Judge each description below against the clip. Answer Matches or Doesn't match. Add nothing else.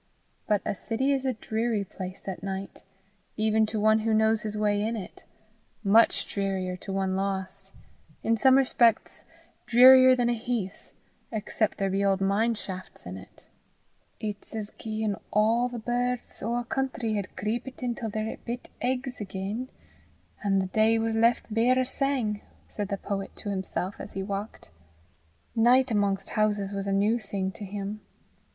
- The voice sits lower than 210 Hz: Doesn't match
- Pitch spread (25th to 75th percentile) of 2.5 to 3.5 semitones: Matches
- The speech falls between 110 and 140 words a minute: Doesn't match